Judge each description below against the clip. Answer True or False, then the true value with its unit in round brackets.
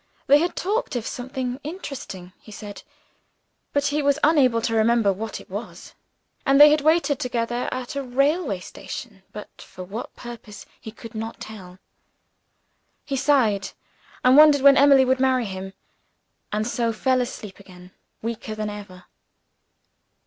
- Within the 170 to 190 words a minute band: False (150 wpm)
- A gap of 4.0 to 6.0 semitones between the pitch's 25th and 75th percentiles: True (4.7 semitones)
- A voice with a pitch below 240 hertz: False (245 Hz)